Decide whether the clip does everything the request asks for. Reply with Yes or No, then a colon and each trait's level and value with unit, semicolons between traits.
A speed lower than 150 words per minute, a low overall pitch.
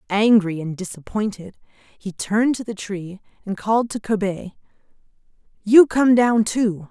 No: average, 140 wpm; high, 205 Hz